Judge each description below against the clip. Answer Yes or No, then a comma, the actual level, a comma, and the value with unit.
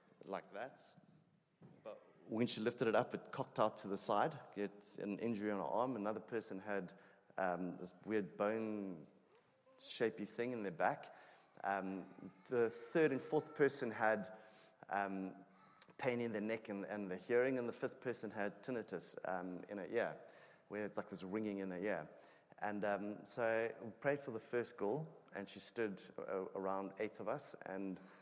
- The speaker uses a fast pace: No, average, 175 wpm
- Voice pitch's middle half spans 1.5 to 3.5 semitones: Yes, average, 2.7 semitones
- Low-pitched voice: Yes, low, 105 Hz